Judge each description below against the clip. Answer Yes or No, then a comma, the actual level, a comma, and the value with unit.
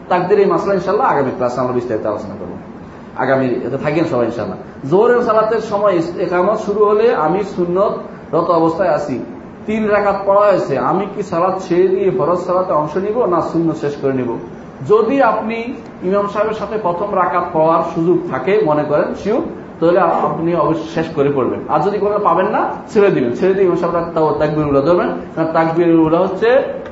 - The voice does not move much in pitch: No, average, 4.3 semitones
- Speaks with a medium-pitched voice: Yes, medium, 180 Hz